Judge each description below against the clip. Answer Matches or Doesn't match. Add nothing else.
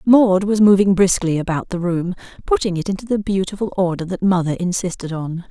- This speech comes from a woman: Matches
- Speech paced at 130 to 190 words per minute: Matches